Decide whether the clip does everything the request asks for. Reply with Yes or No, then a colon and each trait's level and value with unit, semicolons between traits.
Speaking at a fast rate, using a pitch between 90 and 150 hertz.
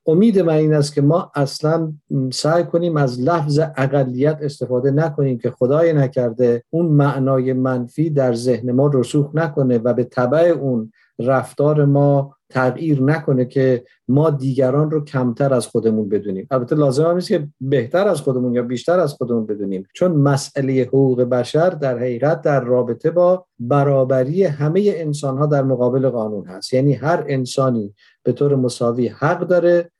Yes: fast, 160 wpm; low, 135 Hz